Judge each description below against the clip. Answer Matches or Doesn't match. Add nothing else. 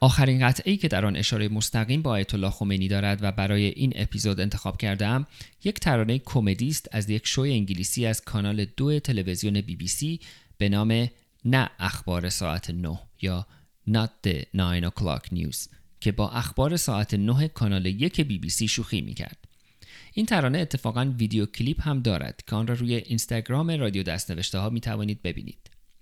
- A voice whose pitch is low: Matches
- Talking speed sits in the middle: Doesn't match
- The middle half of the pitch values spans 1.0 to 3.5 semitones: Doesn't match